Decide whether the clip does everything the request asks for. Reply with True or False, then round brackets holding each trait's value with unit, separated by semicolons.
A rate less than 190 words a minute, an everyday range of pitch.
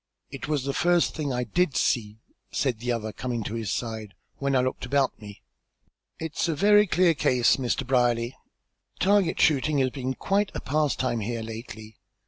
True (175 wpm; 4.7 semitones)